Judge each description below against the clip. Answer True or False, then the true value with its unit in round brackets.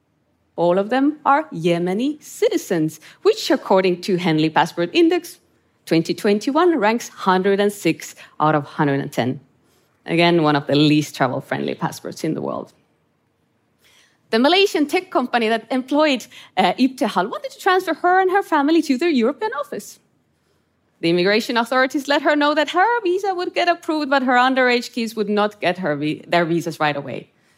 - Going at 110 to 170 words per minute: True (155 wpm)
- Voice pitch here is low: False (230 Hz)